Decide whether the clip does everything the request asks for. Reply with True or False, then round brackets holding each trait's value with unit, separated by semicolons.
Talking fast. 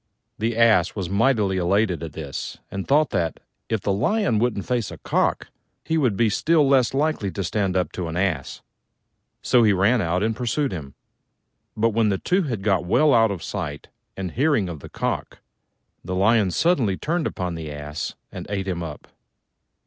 False (185 wpm)